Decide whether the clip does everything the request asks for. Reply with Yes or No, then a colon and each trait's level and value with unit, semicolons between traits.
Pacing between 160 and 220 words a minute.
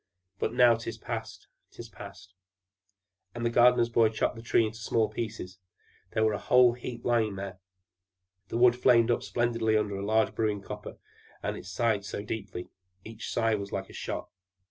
Yes: average, 180 wpm